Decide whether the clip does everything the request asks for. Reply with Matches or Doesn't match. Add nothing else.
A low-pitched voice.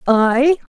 Doesn't match